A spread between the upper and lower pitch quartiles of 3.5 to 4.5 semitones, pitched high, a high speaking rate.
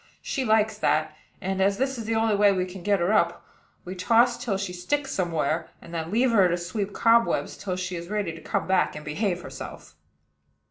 Yes: average, 4.0 semitones; high, 195 Hz; fast, 215 wpm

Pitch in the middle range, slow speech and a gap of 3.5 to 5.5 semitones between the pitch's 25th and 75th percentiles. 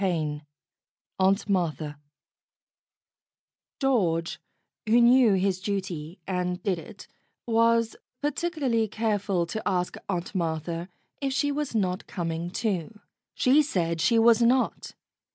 No: high, 195 Hz; slow, 115 wpm; average, 5.1 semitones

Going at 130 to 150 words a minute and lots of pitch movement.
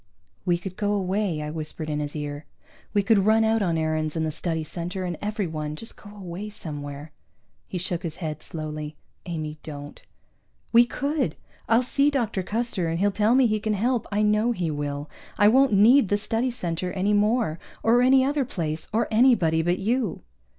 No: average, 190 wpm; wide, 5.9 semitones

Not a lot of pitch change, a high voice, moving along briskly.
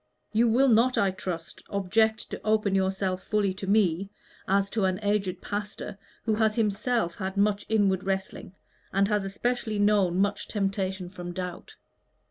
No: narrow, 2.0 semitones; high, 200 Hz; average, 155 wpm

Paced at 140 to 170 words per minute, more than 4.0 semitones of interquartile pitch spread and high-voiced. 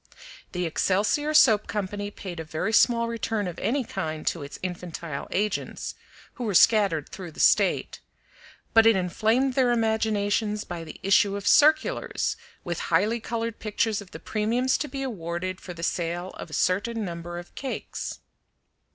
Yes: average, 160 wpm; average, 4.6 semitones; high, 205 Hz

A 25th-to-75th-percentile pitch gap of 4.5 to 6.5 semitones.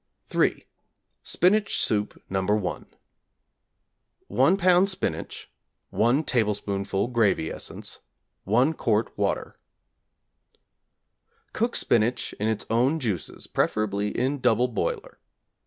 Yes: average, 5.0 semitones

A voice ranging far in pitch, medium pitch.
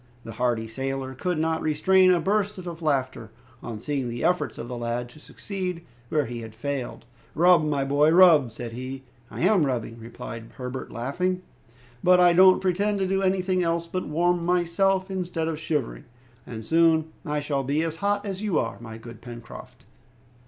Yes: wide, 6.3 semitones; medium, 155 Hz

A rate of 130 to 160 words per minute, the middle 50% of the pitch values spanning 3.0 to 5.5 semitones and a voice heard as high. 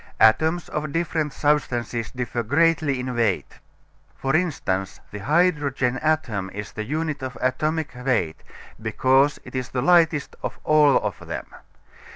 No: average, 140 wpm; average, 4.5 semitones; low, 135 Hz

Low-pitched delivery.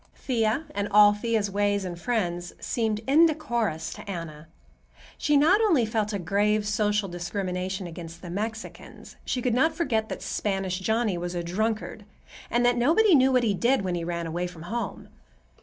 No: high, 210 Hz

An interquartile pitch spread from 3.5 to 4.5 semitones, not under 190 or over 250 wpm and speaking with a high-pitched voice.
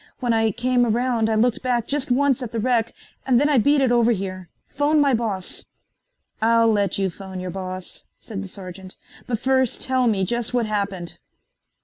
Yes: average, 4.2 semitones; average, 195 wpm; high, 230 Hz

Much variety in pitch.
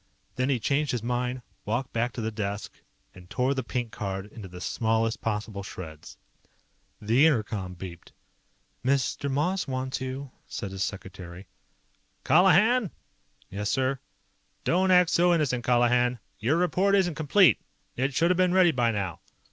Yes: wide, 6.3 semitones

